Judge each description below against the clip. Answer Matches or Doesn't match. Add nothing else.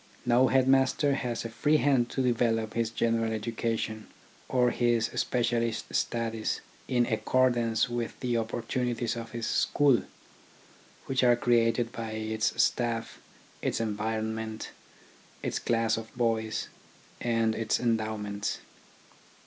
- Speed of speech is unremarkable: Doesn't match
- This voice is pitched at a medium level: Doesn't match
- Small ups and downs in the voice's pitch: Matches